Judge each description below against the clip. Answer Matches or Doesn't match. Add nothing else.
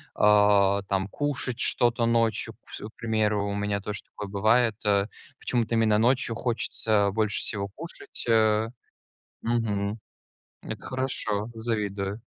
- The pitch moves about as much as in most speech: Doesn't match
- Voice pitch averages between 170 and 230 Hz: Doesn't match